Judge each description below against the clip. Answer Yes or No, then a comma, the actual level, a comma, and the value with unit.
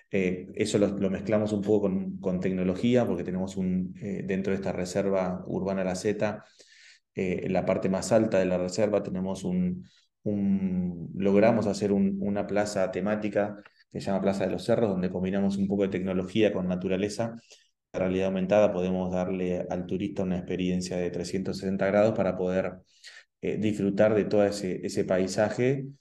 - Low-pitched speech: Yes, very low, 95 Hz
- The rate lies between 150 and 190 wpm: Yes, average, 170 wpm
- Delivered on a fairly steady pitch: Yes, narrow, 2.0 semitones